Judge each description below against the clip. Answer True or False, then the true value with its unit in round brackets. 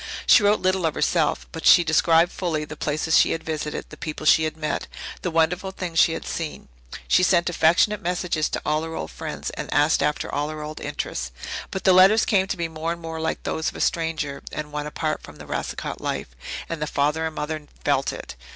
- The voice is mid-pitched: True (160 Hz)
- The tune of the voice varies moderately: False (2.2 semitones)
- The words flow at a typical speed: False (225 wpm)